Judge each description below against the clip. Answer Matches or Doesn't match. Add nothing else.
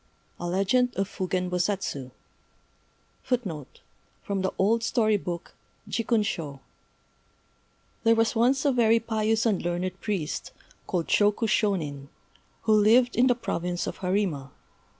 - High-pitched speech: Matches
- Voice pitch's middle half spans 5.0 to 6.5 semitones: Doesn't match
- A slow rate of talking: Matches